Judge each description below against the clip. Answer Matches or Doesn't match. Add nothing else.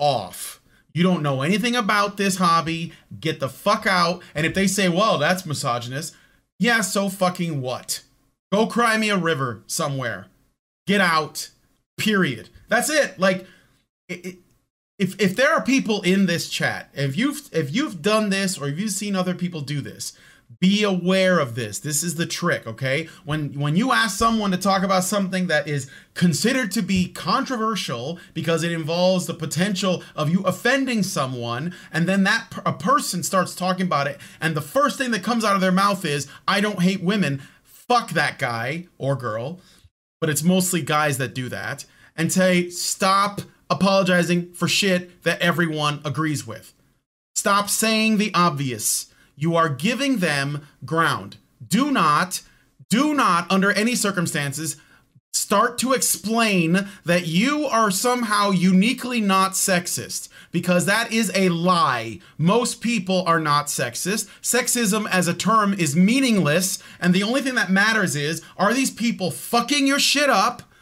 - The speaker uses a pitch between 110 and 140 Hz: Doesn't match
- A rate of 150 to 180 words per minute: Matches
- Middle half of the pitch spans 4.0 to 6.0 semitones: Matches